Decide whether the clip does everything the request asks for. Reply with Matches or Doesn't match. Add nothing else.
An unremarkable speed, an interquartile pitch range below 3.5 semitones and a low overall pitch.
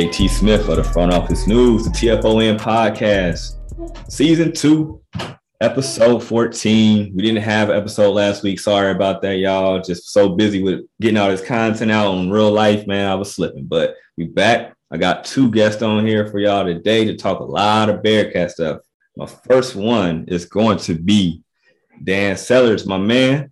Matches